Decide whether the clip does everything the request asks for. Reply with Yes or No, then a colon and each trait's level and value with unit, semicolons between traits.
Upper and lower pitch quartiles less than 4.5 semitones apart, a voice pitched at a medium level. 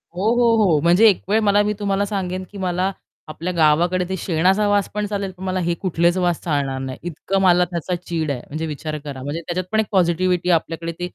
Yes: average, 2.8 semitones; medium, 180 Hz